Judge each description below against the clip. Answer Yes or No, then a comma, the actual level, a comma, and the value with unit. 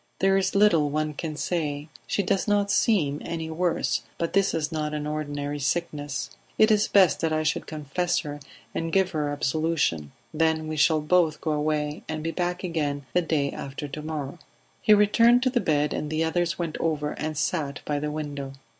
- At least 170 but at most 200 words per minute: Yes, average, 195 wpm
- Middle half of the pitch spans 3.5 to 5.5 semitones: No, average, 3.0 semitones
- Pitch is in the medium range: Yes, medium, 155 Hz